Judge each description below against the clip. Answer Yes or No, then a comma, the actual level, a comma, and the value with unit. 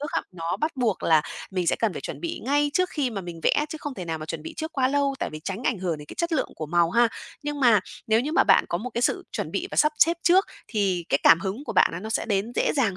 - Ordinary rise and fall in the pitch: No, wide, 8.6 semitones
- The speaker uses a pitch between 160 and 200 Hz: No, high, 225 Hz